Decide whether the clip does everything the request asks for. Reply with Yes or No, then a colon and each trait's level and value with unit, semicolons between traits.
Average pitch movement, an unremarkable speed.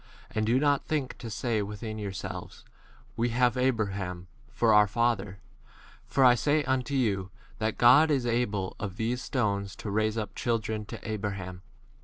Yes: average, 3.4 semitones; average, 165 wpm